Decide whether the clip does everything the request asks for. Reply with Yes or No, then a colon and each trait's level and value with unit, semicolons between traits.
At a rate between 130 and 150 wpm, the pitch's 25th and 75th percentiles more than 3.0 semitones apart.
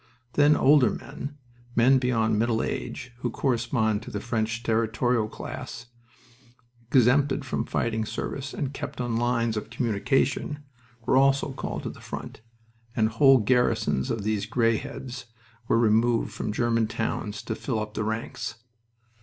No: average, 145 wpm; average, 2.7 semitones